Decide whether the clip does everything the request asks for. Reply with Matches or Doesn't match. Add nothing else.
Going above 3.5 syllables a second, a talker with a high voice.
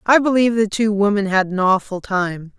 Matches